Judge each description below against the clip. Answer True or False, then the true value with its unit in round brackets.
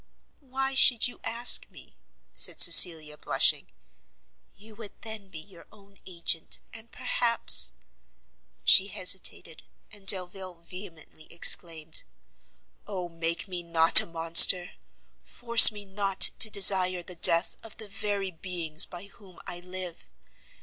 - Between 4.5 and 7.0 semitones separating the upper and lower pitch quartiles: False (3.6 semitones)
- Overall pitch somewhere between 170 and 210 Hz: True (185 Hz)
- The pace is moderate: False (130 wpm)